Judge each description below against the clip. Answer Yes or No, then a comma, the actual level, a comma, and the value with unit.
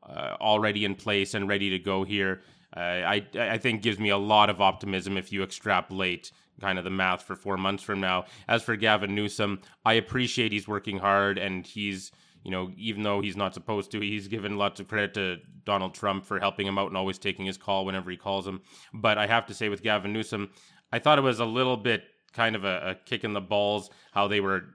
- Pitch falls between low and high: No, low, 100 Hz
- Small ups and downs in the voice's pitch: Yes, narrow, 1.6 semitones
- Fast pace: Yes, fast, 235 wpm